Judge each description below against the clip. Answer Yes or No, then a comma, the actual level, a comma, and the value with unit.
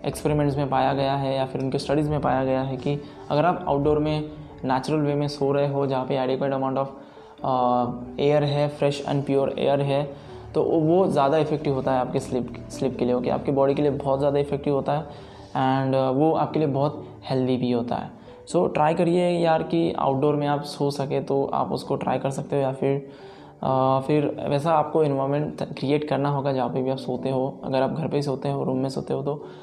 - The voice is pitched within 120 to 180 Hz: Yes, medium, 140 Hz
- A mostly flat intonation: Yes, narrow, 1.7 semitones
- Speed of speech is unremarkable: No, fast, 225 wpm